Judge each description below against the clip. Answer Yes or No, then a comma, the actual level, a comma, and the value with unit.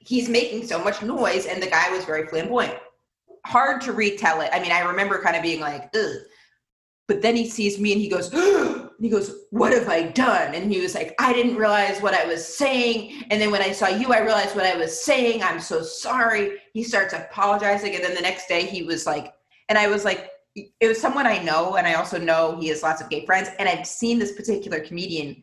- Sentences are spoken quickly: Yes, fast, 240 wpm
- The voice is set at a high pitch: Yes, high, 205 Hz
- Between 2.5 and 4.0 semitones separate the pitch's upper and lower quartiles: No, average, 4.9 semitones